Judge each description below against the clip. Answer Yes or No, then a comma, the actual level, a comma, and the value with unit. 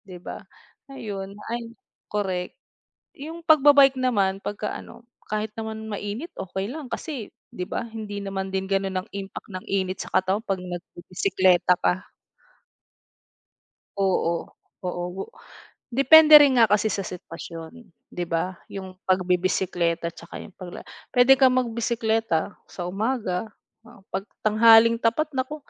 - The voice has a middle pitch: No, high, 200 Hz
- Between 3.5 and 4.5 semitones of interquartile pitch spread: Yes, average, 4.1 semitones